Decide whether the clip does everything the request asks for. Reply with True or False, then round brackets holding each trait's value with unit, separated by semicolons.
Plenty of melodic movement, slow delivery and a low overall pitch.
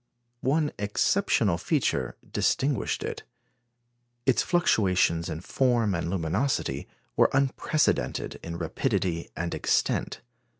True (8.1 semitones; 95 wpm; 100 Hz)